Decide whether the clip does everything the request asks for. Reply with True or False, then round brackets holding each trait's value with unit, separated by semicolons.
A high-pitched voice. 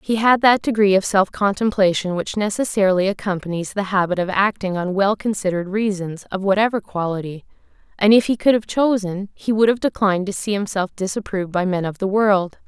True (200 Hz)